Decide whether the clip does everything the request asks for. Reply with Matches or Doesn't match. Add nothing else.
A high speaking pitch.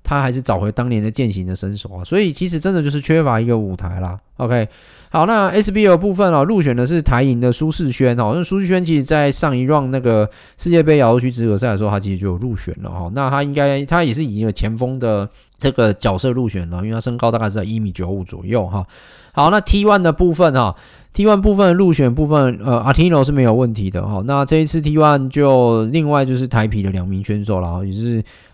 Doesn't match